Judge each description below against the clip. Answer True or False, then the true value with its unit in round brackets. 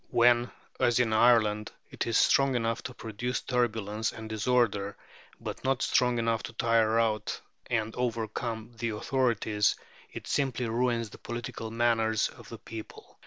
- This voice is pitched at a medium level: False (115 Hz)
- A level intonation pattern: True (1.8 semitones)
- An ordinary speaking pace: True (150 wpm)